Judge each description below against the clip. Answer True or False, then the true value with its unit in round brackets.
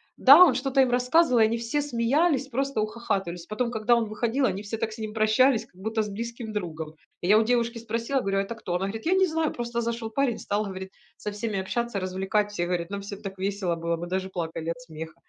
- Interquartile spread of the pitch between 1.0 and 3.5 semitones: False (3.9 semitones)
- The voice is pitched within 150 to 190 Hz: False (220 Hz)